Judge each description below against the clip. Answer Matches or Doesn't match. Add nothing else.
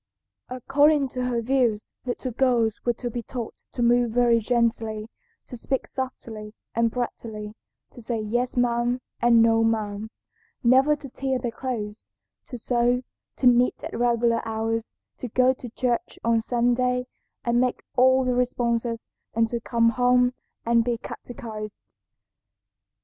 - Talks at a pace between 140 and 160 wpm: Matches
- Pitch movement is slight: Matches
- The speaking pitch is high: Matches